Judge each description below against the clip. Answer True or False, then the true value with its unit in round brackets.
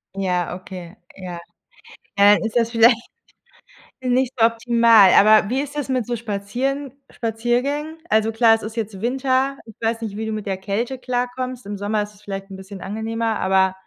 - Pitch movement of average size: True (3.5 semitones)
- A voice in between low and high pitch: False (225 Hz)